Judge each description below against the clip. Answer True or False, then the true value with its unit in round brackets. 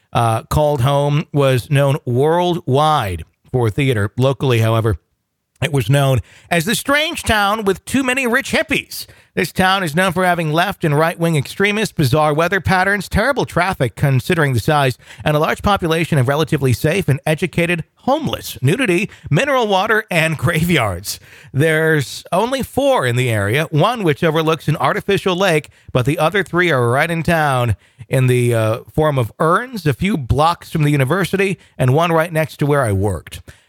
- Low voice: False (155 Hz)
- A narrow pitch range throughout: False (5.2 semitones)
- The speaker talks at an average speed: True (170 wpm)